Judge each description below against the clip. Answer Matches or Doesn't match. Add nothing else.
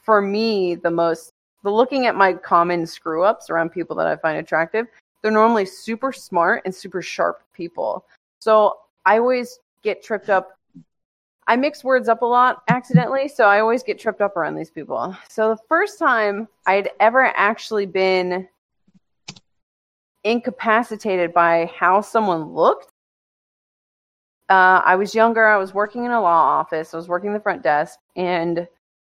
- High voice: Matches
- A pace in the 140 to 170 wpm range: Matches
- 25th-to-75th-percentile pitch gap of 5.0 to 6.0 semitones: Doesn't match